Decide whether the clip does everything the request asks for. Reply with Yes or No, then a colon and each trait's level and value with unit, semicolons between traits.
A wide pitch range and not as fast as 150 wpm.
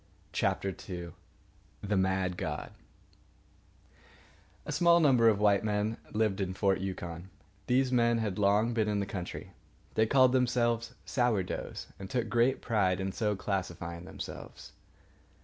No: average, 3.7 semitones; average, 140 wpm